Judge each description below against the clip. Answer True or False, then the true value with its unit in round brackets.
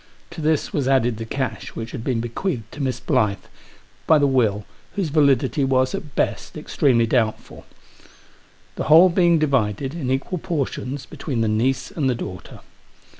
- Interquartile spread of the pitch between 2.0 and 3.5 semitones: False (4.3 semitones)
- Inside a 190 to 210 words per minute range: False (165 wpm)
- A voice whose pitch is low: True (130 Hz)